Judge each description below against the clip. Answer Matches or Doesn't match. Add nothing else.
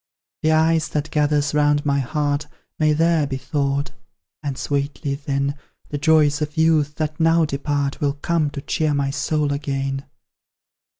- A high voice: Doesn't match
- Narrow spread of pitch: Matches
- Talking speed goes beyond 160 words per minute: Doesn't match